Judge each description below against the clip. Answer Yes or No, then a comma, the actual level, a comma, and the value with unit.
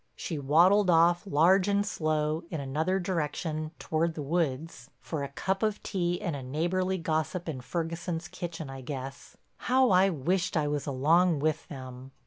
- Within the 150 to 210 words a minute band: Yes, average, 160 wpm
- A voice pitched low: No, medium, 165 Hz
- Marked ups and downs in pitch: No, average, 3.7 semitones